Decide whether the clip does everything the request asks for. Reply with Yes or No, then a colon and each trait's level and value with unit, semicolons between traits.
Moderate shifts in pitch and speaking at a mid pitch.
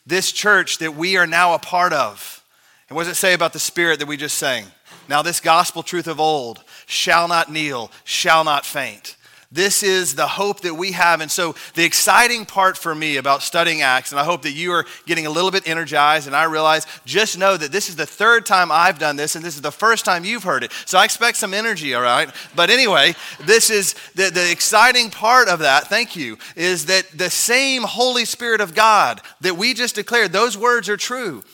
Yes: average, 4.5 semitones; medium, 175 Hz